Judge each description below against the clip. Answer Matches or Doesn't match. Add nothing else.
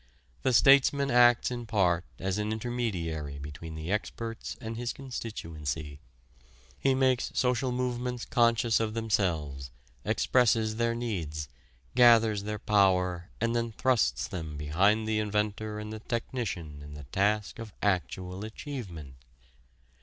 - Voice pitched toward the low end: Matches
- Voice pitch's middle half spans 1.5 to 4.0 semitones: Doesn't match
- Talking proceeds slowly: Matches